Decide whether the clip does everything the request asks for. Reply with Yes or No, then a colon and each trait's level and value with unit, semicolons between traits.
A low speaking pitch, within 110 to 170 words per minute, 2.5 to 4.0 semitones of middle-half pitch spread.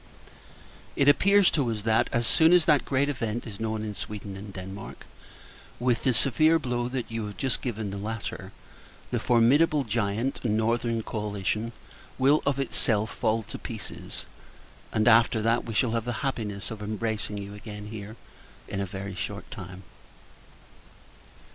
Yes: low, 110 Hz; average, 155 wpm; average, 3.0 semitones